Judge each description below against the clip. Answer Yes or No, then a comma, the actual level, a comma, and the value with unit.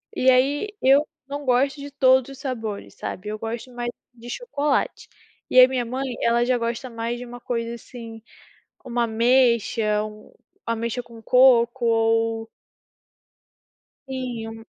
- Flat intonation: Yes, narrow, 2.3 semitones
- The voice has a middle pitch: No, high, 240 Hz